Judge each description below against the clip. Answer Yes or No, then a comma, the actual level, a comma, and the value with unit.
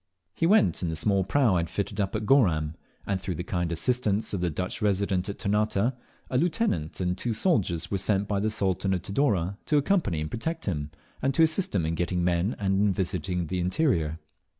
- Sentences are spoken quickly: Yes, fast, 215 wpm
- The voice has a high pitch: No, low, 100 Hz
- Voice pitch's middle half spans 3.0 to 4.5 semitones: Yes, average, 4.0 semitones